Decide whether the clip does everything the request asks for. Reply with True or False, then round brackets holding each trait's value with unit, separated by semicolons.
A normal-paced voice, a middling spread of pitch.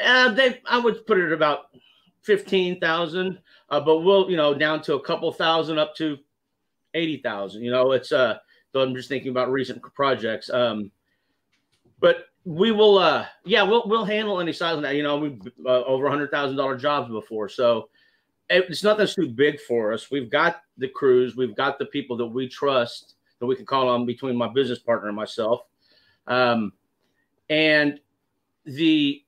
False (180 wpm; 6.4 semitones)